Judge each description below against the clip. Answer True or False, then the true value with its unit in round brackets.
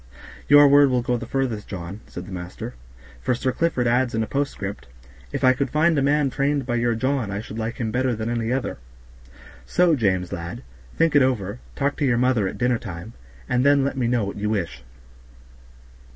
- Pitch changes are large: False (4.2 semitones)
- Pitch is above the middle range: False (125 Hz)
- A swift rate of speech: True (210 wpm)